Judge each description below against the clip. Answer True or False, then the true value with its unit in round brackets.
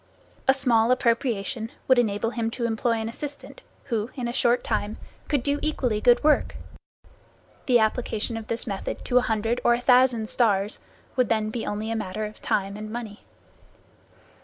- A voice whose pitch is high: True (230 Hz)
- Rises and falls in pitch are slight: True (2.3 semitones)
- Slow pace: False (175 wpm)